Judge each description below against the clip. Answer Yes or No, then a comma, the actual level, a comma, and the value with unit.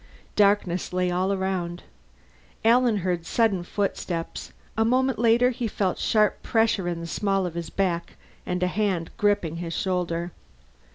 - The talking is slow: No, average, 150 wpm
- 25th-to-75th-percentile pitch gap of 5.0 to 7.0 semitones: No, average, 3.5 semitones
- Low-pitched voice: No, high, 190 Hz